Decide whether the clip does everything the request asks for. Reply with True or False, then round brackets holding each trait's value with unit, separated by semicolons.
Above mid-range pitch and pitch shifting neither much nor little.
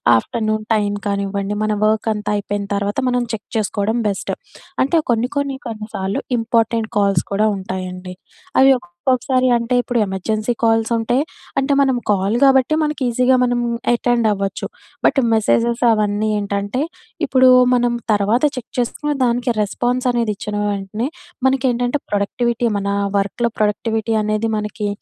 True (220 Hz; 3.1 semitones)